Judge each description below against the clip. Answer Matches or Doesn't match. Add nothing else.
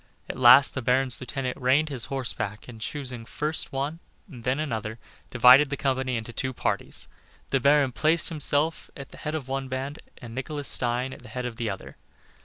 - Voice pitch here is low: Matches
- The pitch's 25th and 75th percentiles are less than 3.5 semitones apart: Matches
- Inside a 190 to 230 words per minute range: Matches